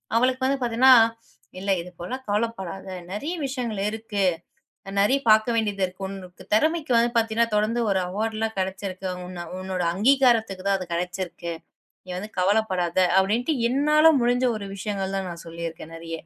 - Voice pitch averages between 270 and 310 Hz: No, high, 210 Hz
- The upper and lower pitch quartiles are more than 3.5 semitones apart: Yes, average, 4.0 semitones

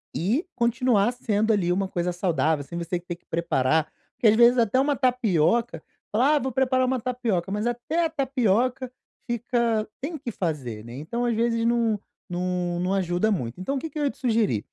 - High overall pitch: Yes, high, 225 Hz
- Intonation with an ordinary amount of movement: No, wide, 6.0 semitones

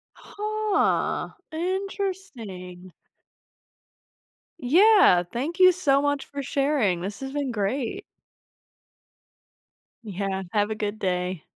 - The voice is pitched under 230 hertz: No, very high, 265 Hz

